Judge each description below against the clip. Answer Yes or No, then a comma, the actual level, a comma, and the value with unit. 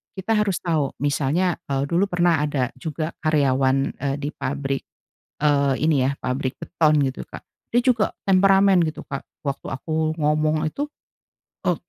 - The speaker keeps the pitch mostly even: No, average, 4.1 semitones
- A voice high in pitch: No, medium, 150 Hz